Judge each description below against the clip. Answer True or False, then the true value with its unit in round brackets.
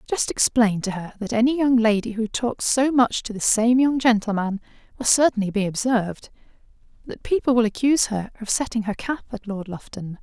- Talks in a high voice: True (225 Hz)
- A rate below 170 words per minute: False (190 wpm)